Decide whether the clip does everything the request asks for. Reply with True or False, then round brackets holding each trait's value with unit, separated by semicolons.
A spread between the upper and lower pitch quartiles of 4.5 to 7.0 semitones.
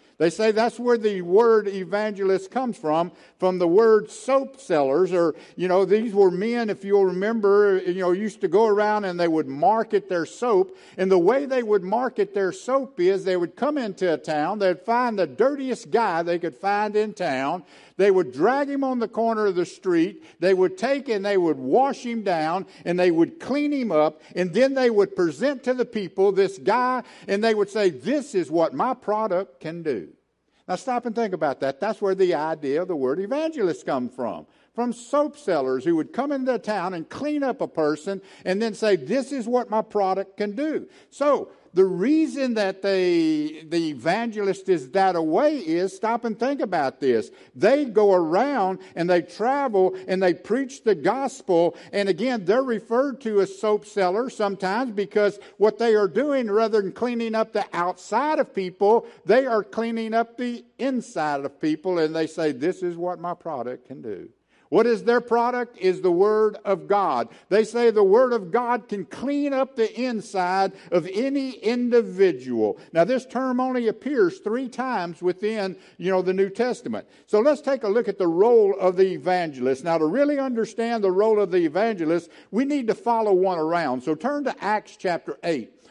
True (4.9 semitones)